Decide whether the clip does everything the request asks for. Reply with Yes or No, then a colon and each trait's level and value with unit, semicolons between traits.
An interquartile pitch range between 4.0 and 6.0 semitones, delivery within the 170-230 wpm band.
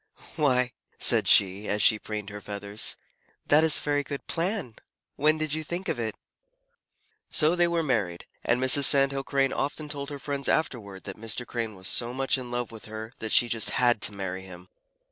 Yes: average, 5.3 semitones; average, 200 wpm